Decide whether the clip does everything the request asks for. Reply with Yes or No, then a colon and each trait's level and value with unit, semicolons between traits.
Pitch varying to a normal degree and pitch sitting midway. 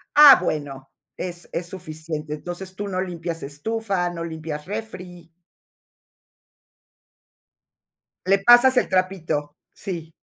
Yes: average, 3.4 semitones; medium, 175 Hz